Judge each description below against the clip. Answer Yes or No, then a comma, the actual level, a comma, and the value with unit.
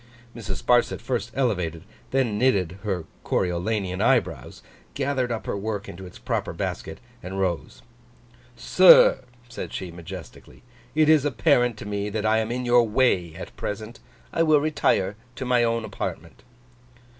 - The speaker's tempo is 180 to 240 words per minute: No, average, 150 wpm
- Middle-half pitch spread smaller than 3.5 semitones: No, average, 4.6 semitones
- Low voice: Yes, low, 110 Hz